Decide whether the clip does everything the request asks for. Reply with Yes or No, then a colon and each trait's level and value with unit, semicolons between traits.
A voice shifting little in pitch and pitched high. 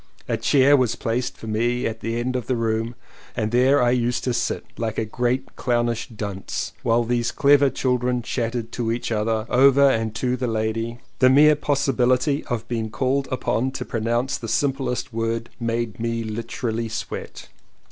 No: narrow, 2.0 semitones; low, 120 Hz